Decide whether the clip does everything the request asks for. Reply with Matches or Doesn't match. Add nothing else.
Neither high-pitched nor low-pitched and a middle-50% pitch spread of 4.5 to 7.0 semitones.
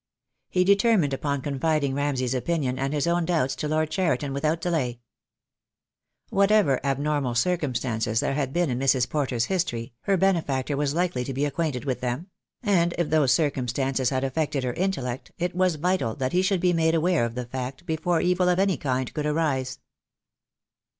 Matches